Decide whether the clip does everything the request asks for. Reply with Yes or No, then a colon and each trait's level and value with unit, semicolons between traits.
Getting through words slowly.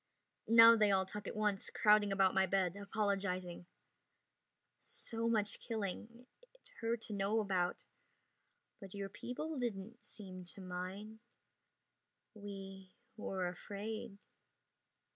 Yes: slow, 115 wpm